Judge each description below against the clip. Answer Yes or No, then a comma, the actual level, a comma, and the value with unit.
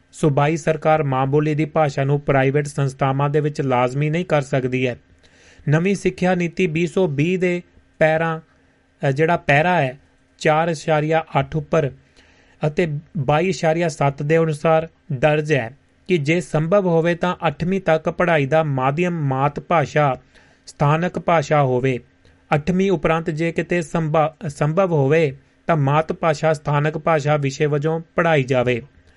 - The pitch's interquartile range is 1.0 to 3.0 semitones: Yes, average, 2.7 semitones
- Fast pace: No, average, 130 wpm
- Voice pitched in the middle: Yes, medium, 155 Hz